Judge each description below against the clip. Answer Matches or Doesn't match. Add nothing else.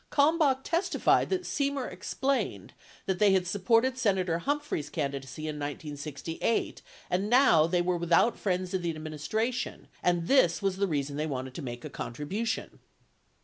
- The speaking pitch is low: Doesn't match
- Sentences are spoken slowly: Doesn't match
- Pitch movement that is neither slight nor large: Doesn't match